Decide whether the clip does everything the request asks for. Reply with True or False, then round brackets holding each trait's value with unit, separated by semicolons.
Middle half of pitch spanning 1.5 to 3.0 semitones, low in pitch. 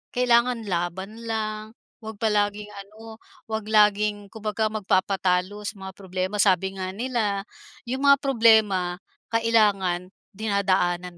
False (2.6 semitones; 210 Hz)